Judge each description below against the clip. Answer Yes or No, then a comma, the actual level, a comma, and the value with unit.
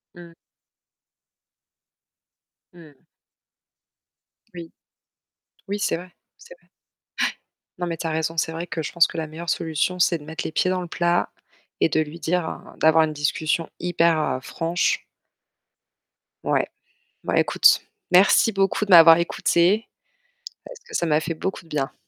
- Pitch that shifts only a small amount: Yes, narrow, 1.9 semitones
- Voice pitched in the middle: Yes, medium, 170 Hz